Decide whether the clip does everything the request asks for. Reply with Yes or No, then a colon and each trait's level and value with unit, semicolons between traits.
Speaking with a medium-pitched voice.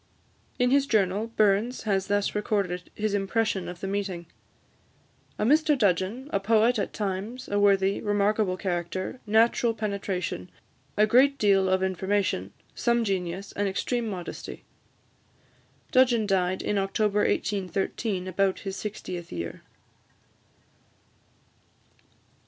No: high, 200 Hz